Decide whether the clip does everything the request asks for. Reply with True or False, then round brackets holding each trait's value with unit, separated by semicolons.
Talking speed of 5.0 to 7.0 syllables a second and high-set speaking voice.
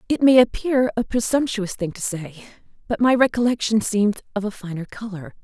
True (5.5 syllables/s; 220 Hz)